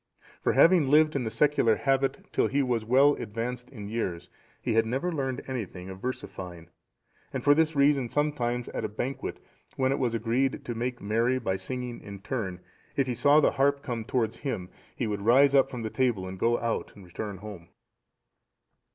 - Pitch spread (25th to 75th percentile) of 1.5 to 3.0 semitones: No, average, 4.1 semitones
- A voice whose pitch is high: No, low, 120 Hz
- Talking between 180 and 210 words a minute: Yes, average, 190 wpm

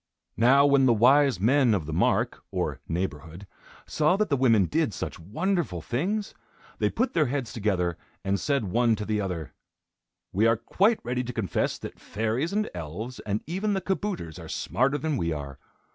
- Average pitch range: No, wide, 7.3 semitones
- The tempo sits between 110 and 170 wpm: No, average, 180 wpm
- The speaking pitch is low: Yes, low, 120 Hz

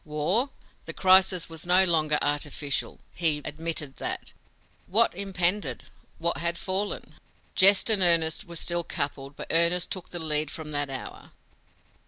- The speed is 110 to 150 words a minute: Yes, average, 145 wpm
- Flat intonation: No, average, 3.7 semitones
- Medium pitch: Yes, medium, 170 Hz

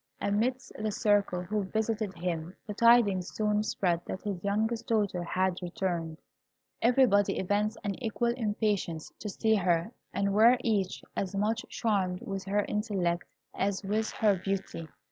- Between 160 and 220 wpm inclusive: No, average, 145 wpm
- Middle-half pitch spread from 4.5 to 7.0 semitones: No, average, 2.8 semitones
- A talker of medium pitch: No, high, 205 Hz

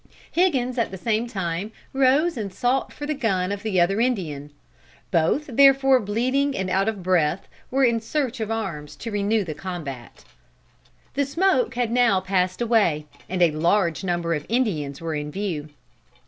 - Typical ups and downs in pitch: No, wide, 6.2 semitones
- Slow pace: No, average, 170 wpm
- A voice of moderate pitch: No, high, 205 Hz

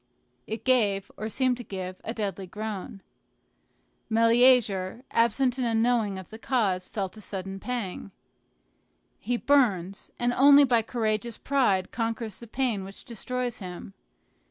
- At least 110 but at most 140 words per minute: Yes, slow, 135 wpm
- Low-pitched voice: No, high, 225 Hz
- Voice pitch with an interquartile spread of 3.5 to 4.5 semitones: Yes, average, 3.9 semitones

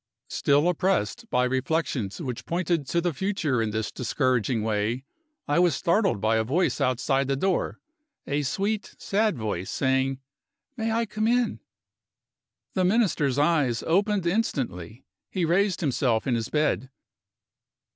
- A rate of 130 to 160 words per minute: Yes, average, 140 wpm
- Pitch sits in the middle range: Yes, medium, 145 Hz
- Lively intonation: Yes, wide, 6.8 semitones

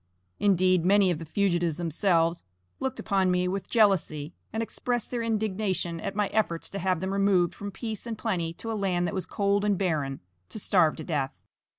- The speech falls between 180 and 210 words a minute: Yes, average, 195 wpm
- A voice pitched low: No, high, 190 Hz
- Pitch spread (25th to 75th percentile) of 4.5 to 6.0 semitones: No, average, 3.2 semitones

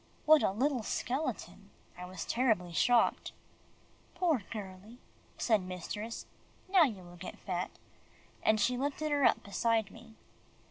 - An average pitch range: No, wide, 5.8 semitones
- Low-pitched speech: No, high, 225 Hz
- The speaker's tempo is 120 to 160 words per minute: Yes, slow, 135 wpm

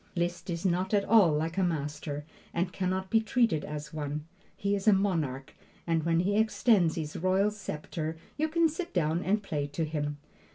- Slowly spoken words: No, average, 195 wpm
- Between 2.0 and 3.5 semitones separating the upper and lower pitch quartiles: No, average, 4.6 semitones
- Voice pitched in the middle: Yes, medium, 175 Hz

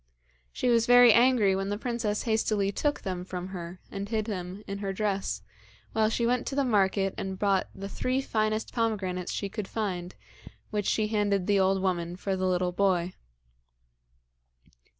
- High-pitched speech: Yes, high, 200 Hz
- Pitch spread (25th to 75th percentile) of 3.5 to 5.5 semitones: No, average, 2.7 semitones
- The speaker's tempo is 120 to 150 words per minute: No, average, 170 wpm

